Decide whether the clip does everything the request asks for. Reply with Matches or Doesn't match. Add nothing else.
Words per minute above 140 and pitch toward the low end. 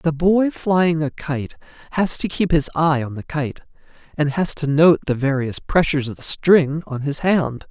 Doesn't match